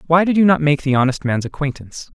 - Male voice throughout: Yes, male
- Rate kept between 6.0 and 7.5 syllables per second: Yes, 6.5 syllables/s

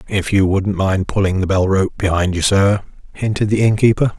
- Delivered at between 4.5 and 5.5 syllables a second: Yes, 5.2 syllables/s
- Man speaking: Yes, male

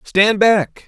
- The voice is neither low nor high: No, high, 205 Hz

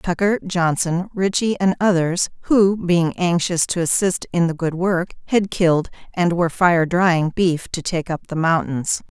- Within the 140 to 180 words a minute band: Yes, average, 170 wpm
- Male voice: No, female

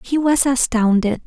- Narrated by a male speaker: No, female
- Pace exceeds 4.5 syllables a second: No, 4.4 syllables/s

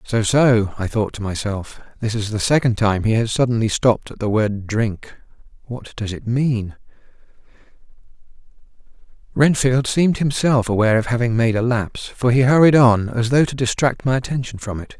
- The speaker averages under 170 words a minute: No, average, 175 wpm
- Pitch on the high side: No, low, 120 Hz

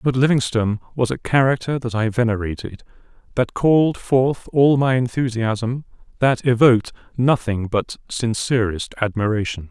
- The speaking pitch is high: No, low, 120 Hz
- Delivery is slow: Yes, slow, 125 wpm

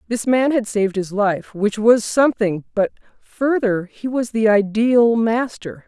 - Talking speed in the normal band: Yes, average, 165 wpm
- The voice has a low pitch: No, high, 220 Hz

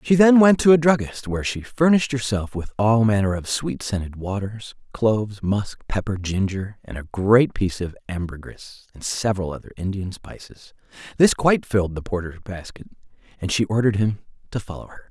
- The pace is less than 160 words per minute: No, average, 180 wpm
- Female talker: No, male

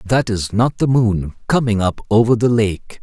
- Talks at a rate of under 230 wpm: Yes, average, 200 wpm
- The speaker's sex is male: Yes, male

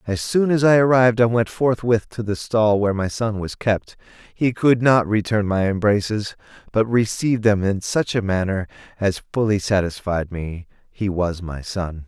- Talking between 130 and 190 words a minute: Yes, average, 185 wpm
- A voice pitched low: Yes, low, 105 Hz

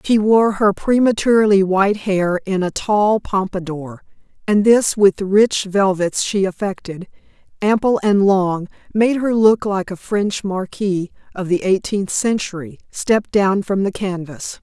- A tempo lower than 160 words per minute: Yes, average, 150 wpm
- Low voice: No, high, 200 Hz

